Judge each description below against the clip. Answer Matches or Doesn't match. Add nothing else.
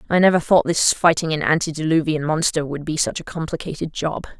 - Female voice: Matches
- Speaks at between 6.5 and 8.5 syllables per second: Doesn't match